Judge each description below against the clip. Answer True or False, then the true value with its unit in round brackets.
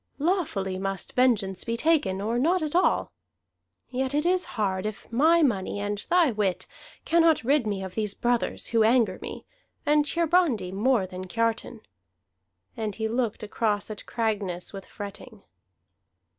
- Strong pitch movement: True (6.2 semitones)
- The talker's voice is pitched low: False (225 Hz)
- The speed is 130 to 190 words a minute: True (150 wpm)